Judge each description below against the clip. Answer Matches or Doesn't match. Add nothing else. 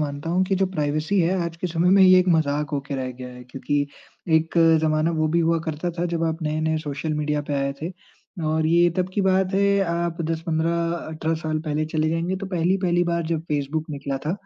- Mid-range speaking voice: Matches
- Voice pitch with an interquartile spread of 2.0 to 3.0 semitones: Matches